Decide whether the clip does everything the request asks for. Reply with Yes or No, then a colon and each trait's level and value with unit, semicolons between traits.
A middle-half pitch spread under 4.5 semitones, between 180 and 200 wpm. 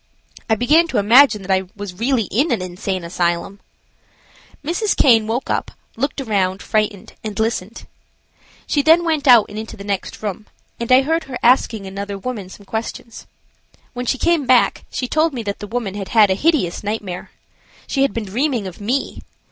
No: average, 4.9 semitones; average, 185 wpm